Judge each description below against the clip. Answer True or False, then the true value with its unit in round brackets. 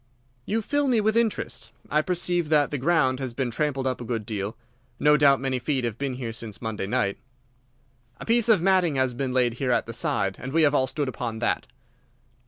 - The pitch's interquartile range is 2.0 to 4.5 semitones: False (5.3 semitones)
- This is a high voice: False (135 Hz)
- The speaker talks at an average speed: False (215 wpm)